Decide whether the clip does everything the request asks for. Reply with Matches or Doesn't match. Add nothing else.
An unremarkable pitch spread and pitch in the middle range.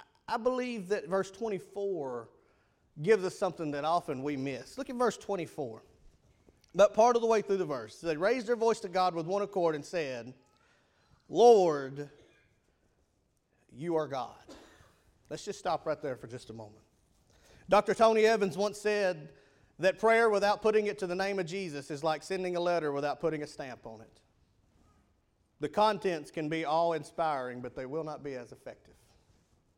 Doesn't match